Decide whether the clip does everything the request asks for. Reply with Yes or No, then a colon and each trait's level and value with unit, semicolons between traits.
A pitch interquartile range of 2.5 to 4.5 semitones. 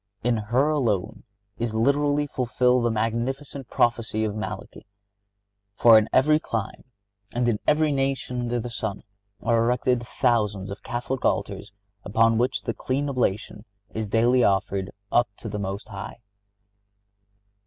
Yes: average, 2.8 semitones